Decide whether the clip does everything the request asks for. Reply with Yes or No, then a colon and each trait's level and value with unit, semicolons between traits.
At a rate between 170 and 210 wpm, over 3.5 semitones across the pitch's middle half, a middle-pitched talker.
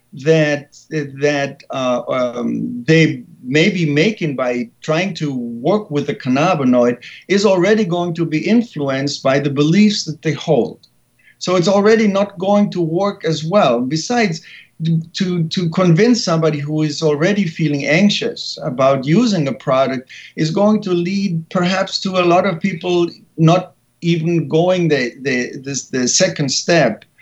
No: average, 150 wpm; average, 4.9 semitones; medium, 165 Hz